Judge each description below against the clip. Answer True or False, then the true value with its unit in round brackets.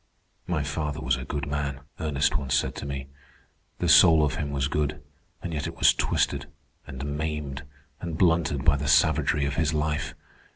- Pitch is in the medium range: False (75 Hz)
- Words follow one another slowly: False (180 wpm)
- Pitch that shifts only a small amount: True (1.8 semitones)